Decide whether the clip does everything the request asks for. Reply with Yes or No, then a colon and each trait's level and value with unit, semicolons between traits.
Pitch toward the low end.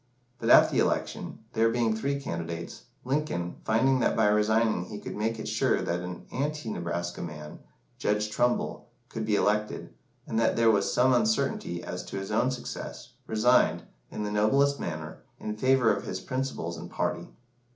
Yes: low, 110 Hz